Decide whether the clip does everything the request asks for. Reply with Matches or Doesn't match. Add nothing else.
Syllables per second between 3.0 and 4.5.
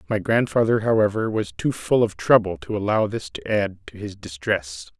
Doesn't match